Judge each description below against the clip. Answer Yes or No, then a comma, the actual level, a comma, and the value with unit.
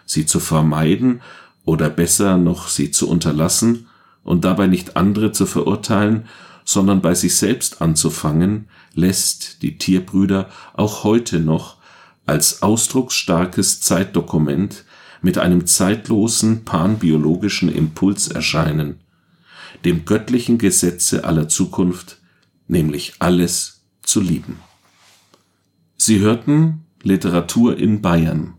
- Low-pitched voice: Yes, very low, 90 Hz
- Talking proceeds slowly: Yes, slow, 105 wpm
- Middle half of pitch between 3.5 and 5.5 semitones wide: Yes, average, 3.8 semitones